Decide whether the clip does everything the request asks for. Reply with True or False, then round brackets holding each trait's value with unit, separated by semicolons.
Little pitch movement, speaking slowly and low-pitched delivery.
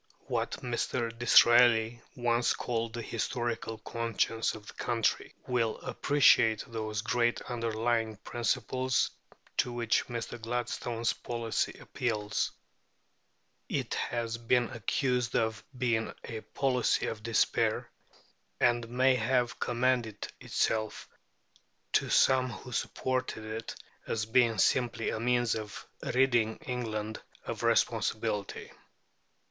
True (1.6 semitones; 110 wpm; 115 Hz)